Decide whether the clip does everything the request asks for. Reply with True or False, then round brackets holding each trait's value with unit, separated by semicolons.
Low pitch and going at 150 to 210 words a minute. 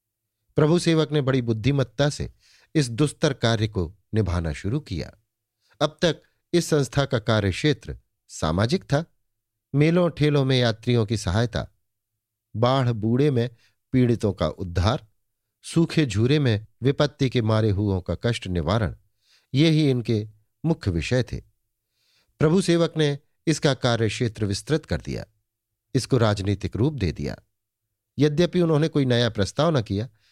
False (115 Hz; 140 wpm)